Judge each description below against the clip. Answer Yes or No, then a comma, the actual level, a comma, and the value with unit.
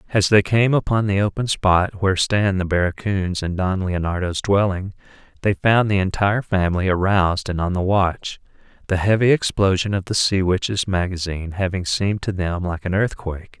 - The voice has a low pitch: Yes, very low, 95 Hz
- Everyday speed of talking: Yes, average, 175 wpm